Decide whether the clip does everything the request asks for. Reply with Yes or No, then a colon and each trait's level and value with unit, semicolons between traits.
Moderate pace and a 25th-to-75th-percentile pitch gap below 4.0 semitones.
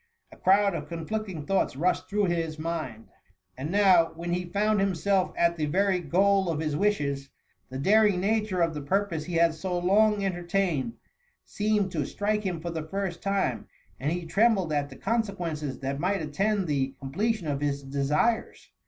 No: average, 180 wpm; average, 4.6 semitones